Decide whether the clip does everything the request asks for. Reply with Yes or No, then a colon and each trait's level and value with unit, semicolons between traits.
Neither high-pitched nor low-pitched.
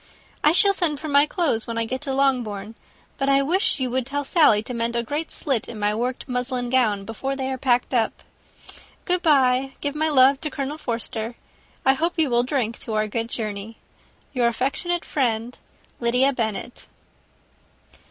No: very high, 255 Hz